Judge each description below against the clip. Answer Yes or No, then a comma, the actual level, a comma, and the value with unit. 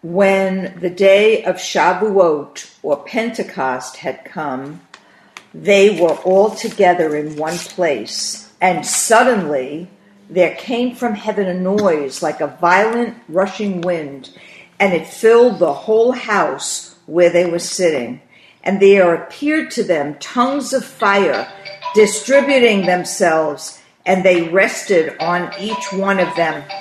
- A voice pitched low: No, high, 195 Hz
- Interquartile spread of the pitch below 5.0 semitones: Yes, average, 3.9 semitones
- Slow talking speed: Yes, slow, 130 wpm